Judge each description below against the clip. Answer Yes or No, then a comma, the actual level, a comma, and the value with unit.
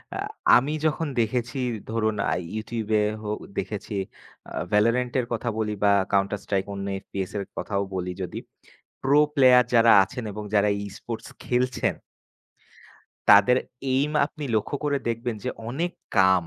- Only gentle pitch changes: No, average, 3.7 semitones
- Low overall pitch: Yes, low, 115 Hz